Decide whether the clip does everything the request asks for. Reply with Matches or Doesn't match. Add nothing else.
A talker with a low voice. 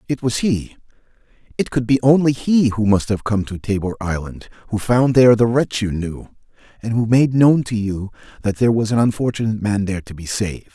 Matches